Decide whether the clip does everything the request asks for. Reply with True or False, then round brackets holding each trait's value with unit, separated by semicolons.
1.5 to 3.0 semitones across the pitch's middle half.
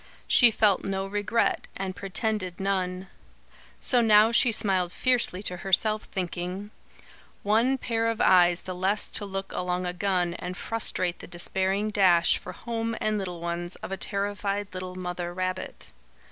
True (2.7 semitones)